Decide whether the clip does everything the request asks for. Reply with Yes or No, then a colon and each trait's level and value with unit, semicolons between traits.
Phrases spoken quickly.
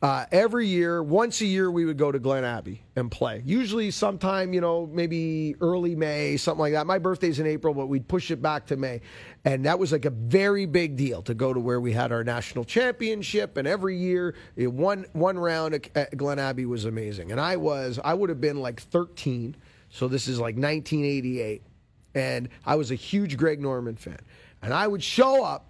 Yes: fast, 210 wpm